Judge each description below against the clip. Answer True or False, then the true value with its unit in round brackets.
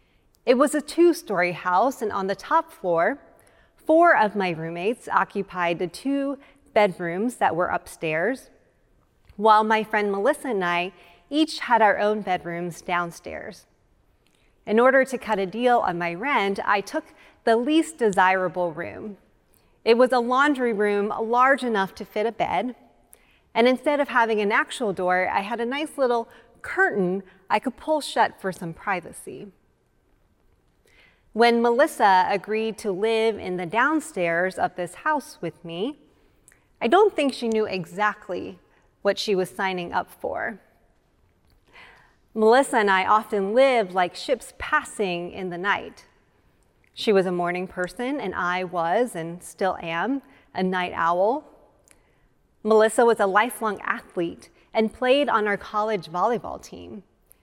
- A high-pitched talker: True (215 Hz)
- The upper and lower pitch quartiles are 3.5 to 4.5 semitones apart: False (5.3 semitones)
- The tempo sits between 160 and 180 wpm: False (150 wpm)